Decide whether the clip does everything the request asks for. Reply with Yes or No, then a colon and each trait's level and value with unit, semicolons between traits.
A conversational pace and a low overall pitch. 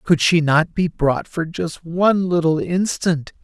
No: average, 175 wpm; medium, 165 Hz